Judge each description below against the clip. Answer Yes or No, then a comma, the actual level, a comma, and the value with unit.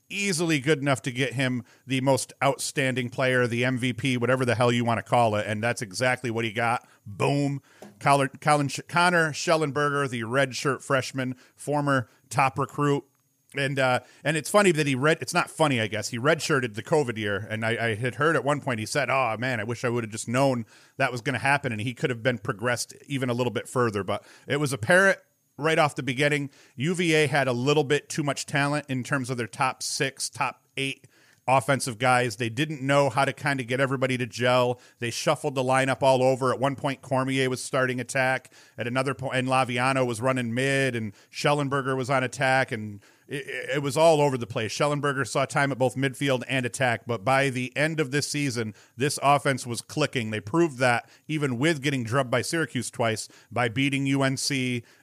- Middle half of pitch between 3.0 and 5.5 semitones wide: No, narrow, 2.4 semitones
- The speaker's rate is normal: No, fast, 210 wpm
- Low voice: Yes, low, 130 Hz